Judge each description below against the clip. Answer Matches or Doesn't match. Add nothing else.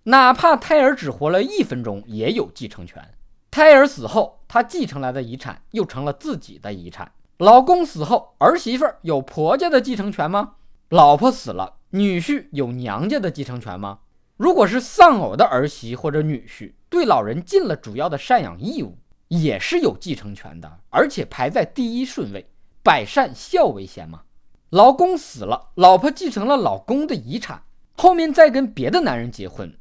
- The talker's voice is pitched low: Doesn't match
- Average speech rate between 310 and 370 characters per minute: Doesn't match